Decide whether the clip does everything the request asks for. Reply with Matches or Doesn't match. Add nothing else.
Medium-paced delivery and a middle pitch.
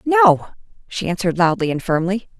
Doesn't match